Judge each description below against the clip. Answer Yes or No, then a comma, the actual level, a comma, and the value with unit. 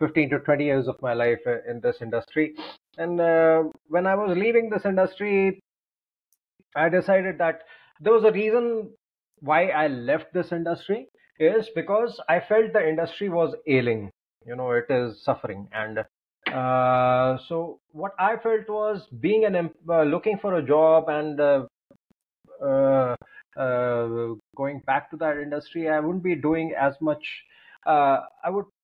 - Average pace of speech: Yes, average, 155 wpm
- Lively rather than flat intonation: Yes, wide, 6.6 semitones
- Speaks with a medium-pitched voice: Yes, medium, 160 Hz